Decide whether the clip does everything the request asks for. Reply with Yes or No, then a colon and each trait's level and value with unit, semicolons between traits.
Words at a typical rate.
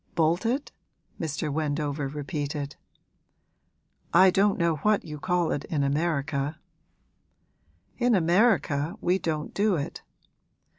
No: slow, 105 wpm